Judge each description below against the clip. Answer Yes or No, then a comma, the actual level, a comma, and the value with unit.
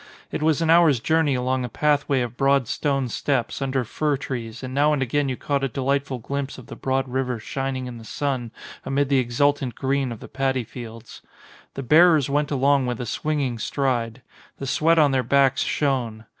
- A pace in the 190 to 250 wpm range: Yes, average, 200 wpm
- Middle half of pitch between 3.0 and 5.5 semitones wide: No, narrow, 2.4 semitones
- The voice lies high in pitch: No, low, 135 Hz